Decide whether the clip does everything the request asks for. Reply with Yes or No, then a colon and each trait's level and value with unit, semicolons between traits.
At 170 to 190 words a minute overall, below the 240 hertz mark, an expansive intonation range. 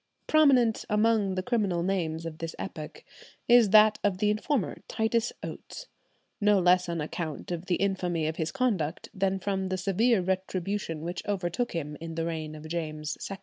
No: average, 175 wpm; medium, 185 Hz; average, 4.2 semitones